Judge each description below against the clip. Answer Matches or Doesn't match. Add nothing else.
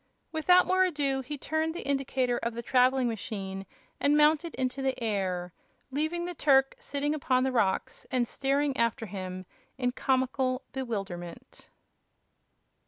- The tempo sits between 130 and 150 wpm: Matches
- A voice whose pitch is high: Matches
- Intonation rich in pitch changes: Doesn't match